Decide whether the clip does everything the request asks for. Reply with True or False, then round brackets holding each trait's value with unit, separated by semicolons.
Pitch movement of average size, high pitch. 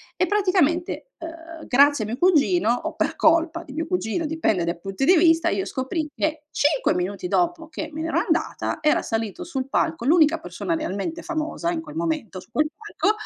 True (3.8 semitones; 320 Hz)